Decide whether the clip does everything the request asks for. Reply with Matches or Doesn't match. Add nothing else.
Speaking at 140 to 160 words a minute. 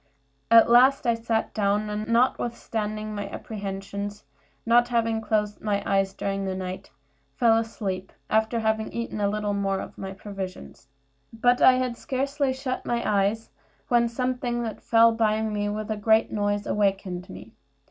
Matches